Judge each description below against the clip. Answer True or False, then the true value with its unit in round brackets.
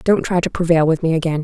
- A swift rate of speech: True (290 wpm)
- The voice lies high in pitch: False (165 Hz)